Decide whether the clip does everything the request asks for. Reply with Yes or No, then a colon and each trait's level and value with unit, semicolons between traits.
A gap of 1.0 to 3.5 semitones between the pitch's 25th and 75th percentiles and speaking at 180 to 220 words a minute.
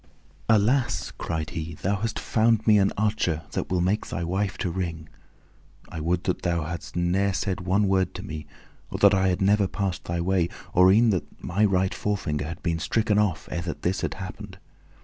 Yes: average, 3.0 semitones; average, 200 wpm